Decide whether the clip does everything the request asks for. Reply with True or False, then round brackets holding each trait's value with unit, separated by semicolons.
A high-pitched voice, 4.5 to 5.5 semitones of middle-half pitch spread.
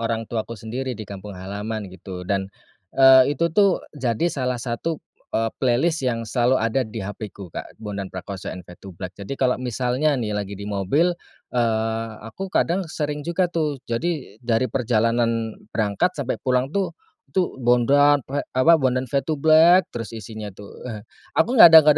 False (120 Hz; 4.9 semitones)